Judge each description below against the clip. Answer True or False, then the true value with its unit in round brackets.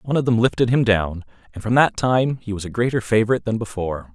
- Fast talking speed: True (245 wpm)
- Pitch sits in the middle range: False (110 Hz)